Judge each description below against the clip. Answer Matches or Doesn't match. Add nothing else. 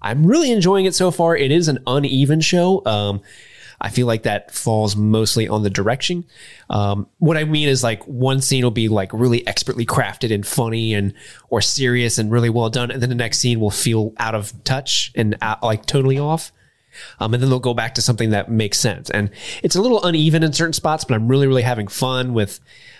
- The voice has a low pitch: Matches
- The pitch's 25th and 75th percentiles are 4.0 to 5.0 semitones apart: Matches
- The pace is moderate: Doesn't match